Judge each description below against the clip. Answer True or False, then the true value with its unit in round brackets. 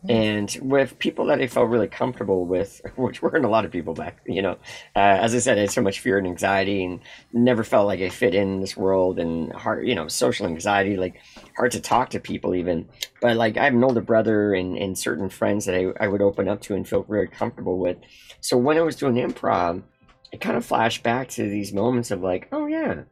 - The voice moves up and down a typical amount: True (4.4 semitones)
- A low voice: True (105 Hz)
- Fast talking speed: True (240 wpm)